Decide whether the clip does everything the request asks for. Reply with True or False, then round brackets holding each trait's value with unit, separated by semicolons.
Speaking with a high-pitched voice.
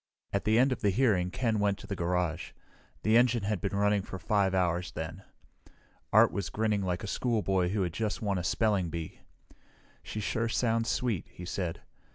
False (100 Hz)